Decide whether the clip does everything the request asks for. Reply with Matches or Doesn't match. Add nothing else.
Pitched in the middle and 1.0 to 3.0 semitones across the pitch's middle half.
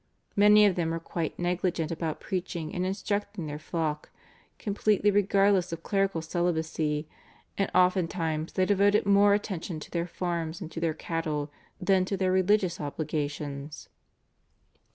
Doesn't match